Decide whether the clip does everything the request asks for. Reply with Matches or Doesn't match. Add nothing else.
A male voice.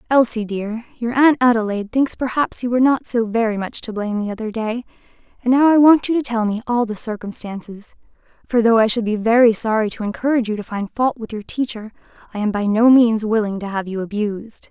Doesn't match